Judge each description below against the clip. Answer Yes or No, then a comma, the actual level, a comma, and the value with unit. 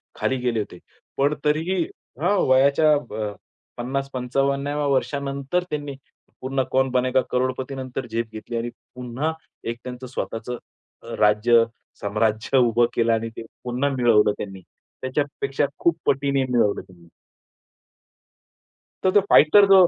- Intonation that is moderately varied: Yes, average, 3.2 semitones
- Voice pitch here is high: No, low, 130 Hz